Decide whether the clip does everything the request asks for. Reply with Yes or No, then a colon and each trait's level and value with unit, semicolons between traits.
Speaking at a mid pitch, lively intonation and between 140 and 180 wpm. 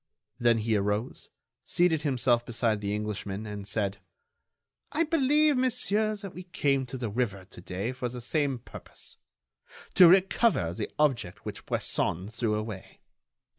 No: low, 120 Hz; wide, 8.9 semitones; average, 145 wpm